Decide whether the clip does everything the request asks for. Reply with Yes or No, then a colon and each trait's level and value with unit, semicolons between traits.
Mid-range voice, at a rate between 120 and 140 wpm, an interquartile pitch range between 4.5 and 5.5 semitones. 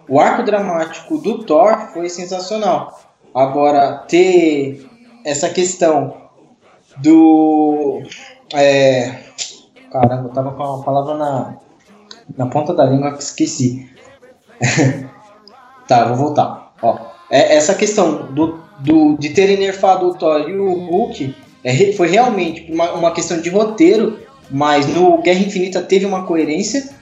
Yes: medium, 165 Hz; average, 130 wpm; average, 5.1 semitones